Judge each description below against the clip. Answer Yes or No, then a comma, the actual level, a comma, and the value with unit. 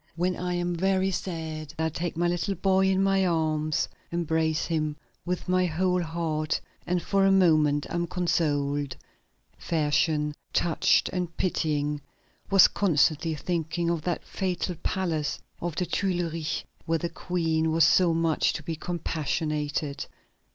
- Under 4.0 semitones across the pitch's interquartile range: Yes, narrow, 2.5 semitones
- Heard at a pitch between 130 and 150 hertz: No, medium, 165 Hz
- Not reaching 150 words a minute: Yes, average, 140 wpm